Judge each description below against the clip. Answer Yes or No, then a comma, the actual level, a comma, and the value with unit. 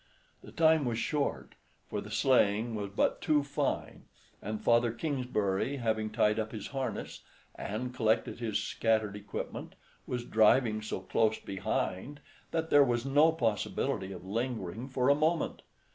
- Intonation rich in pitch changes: No, average, 4.1 semitones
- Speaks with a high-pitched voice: No, low, 115 Hz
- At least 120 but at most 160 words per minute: Yes, average, 145 wpm